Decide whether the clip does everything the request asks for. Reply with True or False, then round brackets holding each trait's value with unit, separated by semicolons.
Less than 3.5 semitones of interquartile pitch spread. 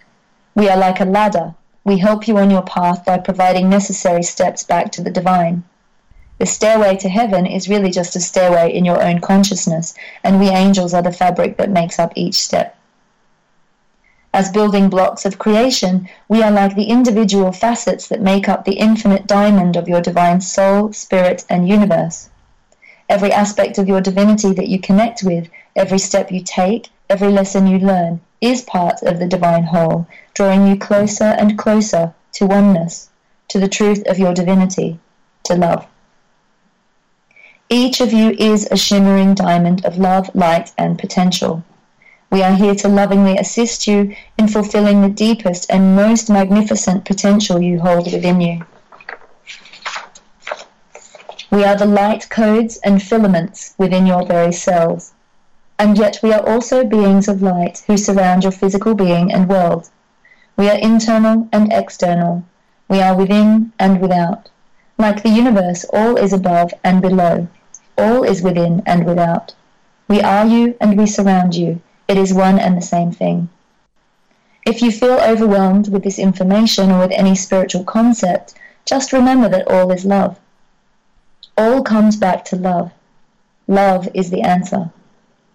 True (2.5 semitones)